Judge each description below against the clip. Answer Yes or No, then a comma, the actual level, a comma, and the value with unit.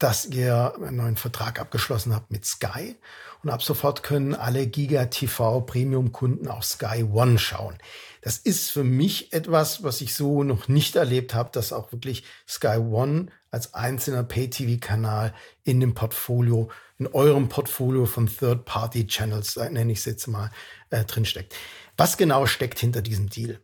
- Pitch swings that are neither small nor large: Yes, average, 3.0 semitones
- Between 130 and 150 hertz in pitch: No, low, 120 Hz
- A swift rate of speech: No, average, 160 wpm